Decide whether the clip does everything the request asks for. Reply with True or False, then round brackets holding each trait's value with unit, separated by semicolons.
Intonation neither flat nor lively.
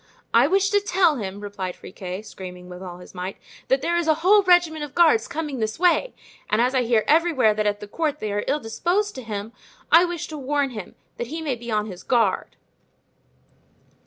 False (7.8 semitones)